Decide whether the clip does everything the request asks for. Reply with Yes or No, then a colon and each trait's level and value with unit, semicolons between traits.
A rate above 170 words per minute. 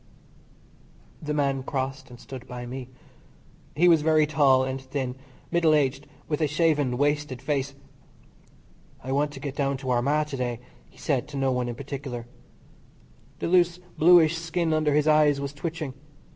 No: average, 165 wpm